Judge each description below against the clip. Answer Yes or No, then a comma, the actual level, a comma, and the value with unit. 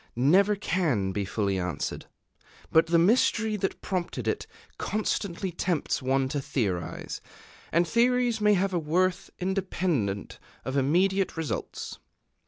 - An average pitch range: No, wide, 6.7 semitones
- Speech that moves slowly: Yes, slow, 125 wpm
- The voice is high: No, medium, 170 Hz